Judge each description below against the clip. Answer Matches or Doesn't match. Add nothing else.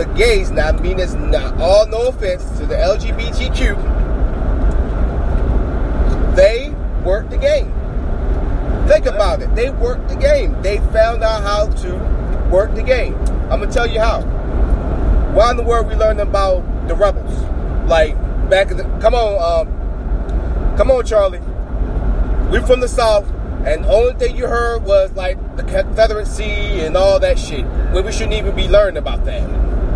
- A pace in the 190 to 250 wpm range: Doesn't match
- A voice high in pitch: Matches